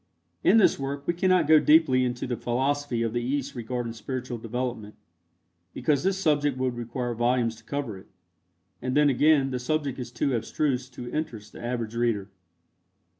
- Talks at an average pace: Yes, average, 175 wpm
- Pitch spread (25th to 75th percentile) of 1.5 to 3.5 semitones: Yes, average, 3.2 semitones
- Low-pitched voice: Yes, low, 125 Hz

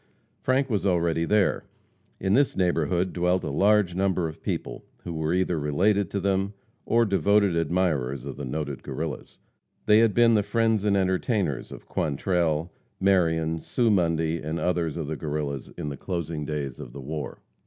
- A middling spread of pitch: Yes, average, 4.2 semitones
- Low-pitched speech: Yes, very low, 85 Hz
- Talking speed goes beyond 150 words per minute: Yes, average, 170 wpm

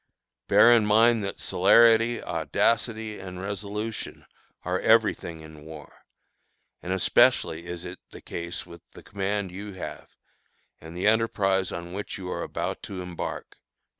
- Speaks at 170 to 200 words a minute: No, average, 145 wpm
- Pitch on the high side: No, very low, 95 Hz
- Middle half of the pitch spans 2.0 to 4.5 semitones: Yes, average, 3.6 semitones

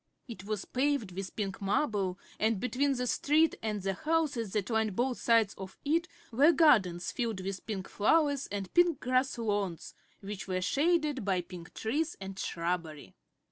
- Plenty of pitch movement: Yes, wide, 6.5 semitones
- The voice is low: No, high, 220 Hz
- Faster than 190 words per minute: No, average, 165 wpm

